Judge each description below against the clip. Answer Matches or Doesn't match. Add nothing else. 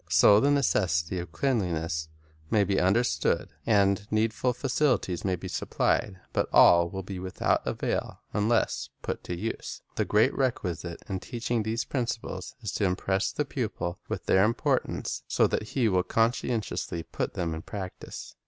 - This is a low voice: Matches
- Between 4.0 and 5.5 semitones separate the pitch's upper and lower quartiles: Matches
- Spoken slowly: Doesn't match